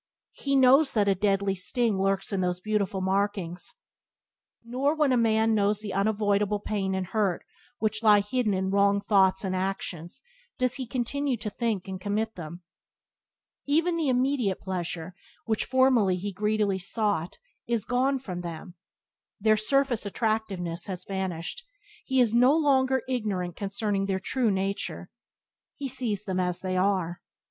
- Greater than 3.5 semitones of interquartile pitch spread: Yes, average, 4.1 semitones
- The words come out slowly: No, average, 155 wpm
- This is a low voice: No, high, 205 Hz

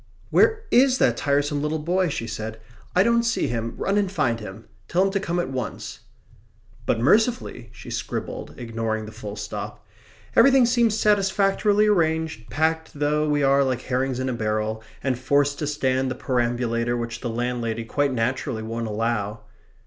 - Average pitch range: No, wide, 6.8 semitones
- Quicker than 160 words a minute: Yes, average, 170 wpm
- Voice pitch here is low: Yes, low, 130 Hz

